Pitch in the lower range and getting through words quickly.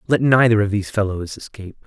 No: low, 105 Hz; average, 195 wpm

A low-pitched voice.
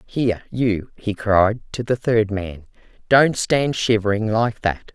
Yes: low, 110 Hz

